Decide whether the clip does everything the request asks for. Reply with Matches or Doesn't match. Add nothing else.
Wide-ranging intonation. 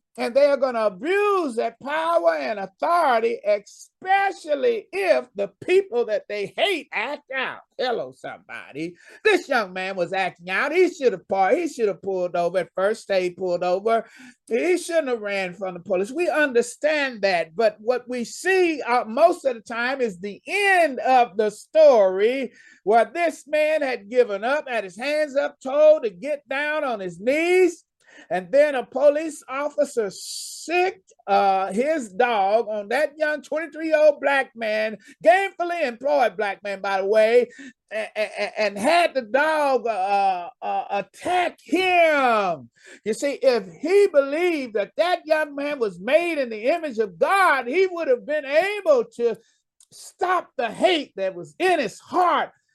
Matches